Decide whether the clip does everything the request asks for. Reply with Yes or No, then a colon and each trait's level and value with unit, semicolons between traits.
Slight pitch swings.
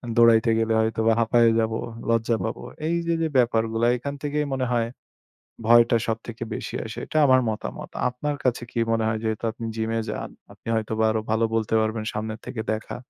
Yes: narrow, 1.5 semitones